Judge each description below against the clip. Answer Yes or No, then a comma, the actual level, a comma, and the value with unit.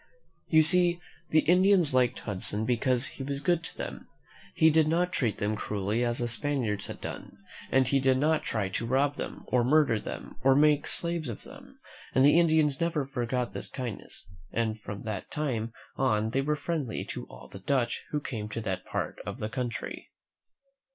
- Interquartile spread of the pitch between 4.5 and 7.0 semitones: Yes, average, 5.0 semitones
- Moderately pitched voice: No, low, 130 Hz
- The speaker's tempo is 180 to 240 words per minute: Yes, average, 190 wpm